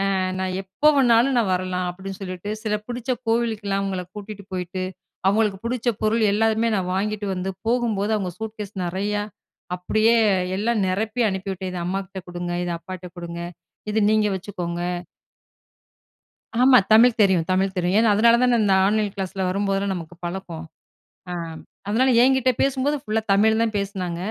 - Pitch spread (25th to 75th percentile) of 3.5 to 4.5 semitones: No, average, 3.1 semitones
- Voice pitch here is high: Yes, high, 200 Hz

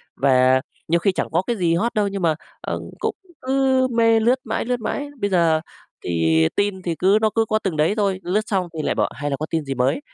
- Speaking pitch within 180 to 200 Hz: Yes, medium, 185 Hz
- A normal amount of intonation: No, wide, 6.1 semitones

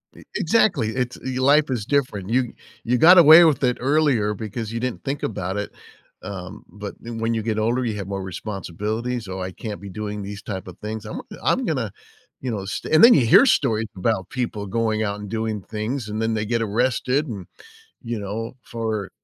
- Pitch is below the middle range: Yes, low, 110 Hz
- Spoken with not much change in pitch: No, average, 3.5 semitones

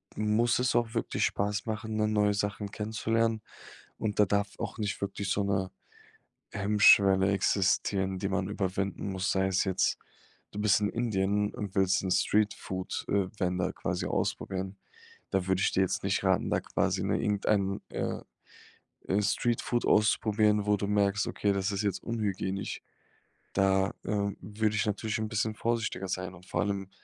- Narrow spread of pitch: Yes, narrow, 1.9 semitones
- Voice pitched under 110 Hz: Yes, low, 100 Hz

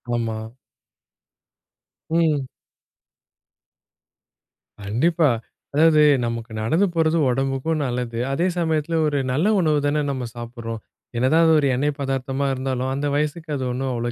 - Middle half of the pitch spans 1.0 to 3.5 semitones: No, average, 4.1 semitones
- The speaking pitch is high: No, low, 135 Hz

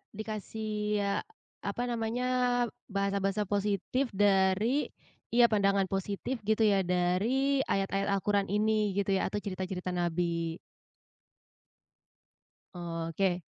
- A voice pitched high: Yes, high, 200 Hz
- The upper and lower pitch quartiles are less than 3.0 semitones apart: Yes, narrow, 2.5 semitones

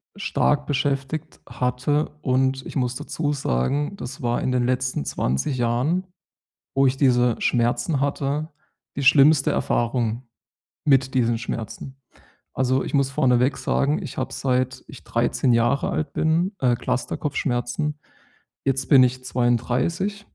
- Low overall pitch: Yes, low, 130 Hz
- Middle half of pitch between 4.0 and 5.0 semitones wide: No, average, 2.9 semitones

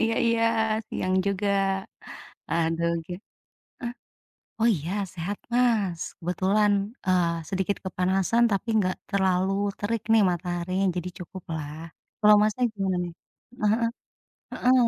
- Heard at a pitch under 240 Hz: Yes, high, 190 Hz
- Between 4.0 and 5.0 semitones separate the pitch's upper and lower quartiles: No, average, 3.2 semitones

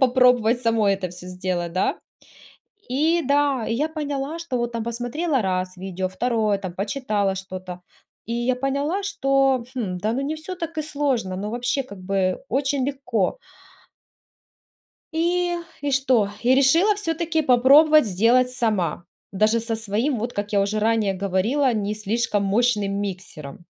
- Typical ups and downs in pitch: No, wide, 5.7 semitones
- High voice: Yes, high, 235 Hz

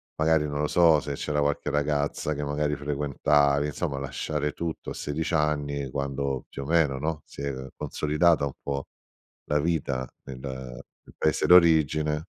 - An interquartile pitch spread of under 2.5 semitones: Yes, narrow, 1.6 semitones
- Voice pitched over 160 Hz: No, very low, 75 Hz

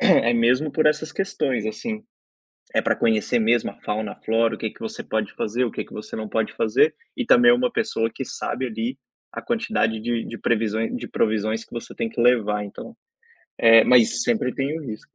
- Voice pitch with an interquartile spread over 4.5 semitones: Yes, wide, 5.4 semitones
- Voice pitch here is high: No, low, 115 Hz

